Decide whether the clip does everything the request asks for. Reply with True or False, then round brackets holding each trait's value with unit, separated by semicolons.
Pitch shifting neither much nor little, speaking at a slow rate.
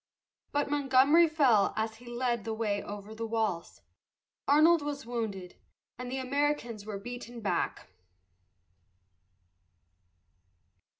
True (4.5 semitones; 110 wpm)